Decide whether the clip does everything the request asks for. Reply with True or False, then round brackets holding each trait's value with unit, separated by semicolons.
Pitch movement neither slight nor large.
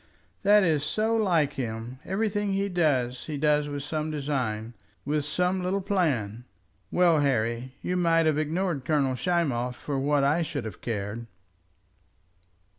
False (5.7 semitones)